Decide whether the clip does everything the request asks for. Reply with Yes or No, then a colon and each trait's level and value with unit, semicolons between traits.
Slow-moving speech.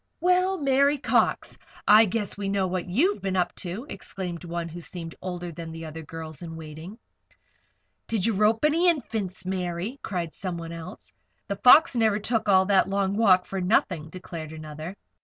No: average, 175 wpm